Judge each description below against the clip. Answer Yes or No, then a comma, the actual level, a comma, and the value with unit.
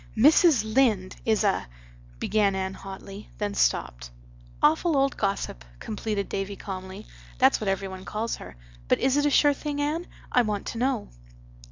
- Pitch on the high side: Yes, high, 215 Hz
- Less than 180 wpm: Yes, average, 165 wpm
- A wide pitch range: Yes, wide, 5.7 semitones